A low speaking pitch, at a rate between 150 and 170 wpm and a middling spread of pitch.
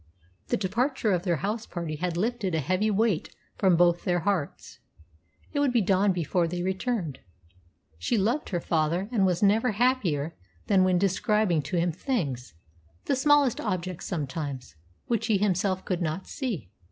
No: medium, 185 Hz; average, 165 wpm; average, 4.2 semitones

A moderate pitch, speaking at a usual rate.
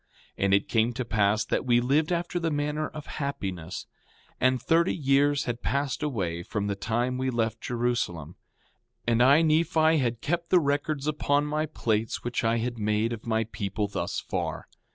No: low, 125 Hz; average, 190 wpm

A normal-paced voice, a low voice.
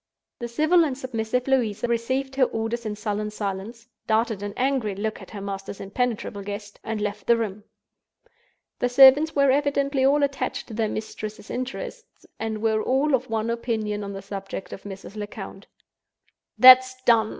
No: average, 160 wpm; high, 225 Hz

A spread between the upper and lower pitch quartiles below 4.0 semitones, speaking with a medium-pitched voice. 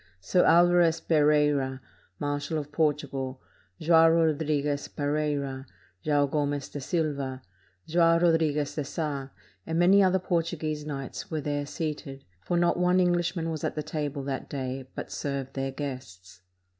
Yes: average, 2.8 semitones; medium, 150 Hz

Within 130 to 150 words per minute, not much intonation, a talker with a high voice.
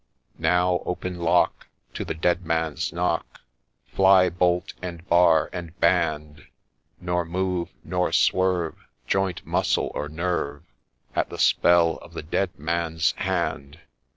No: slow, 135 wpm; narrow, 1.9 semitones; very low, 85 Hz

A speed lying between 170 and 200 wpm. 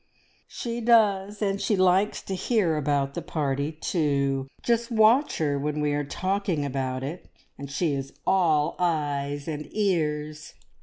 No: average, 150 wpm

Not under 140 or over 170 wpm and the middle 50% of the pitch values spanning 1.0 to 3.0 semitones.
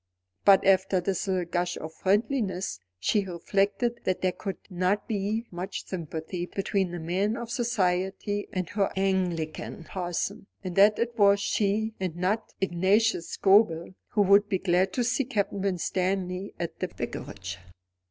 Yes: average, 150 wpm; narrow, 2.5 semitones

